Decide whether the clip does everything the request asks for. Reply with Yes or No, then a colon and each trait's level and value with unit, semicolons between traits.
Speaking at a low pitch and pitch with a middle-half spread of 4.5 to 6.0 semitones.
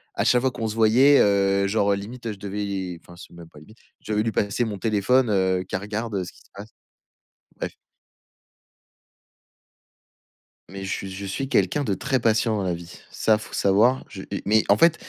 No: low, 105 Hz; average, 2.9 semitones